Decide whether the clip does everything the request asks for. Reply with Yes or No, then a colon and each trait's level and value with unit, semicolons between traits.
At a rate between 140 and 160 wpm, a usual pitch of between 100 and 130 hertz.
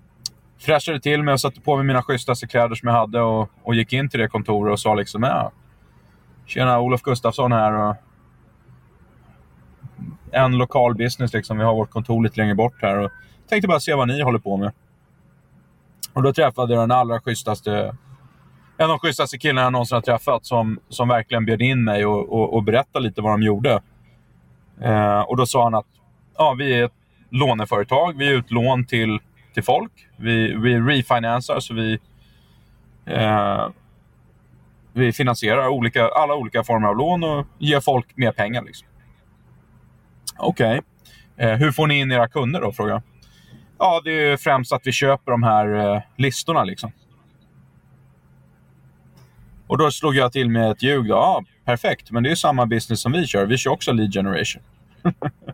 No: average, 175 wpm; low, 120 Hz